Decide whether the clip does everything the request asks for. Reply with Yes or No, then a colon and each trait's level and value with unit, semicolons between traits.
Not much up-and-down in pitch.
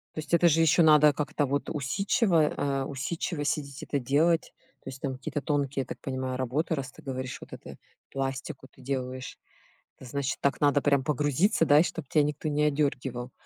Yes: narrow, 2.3 semitones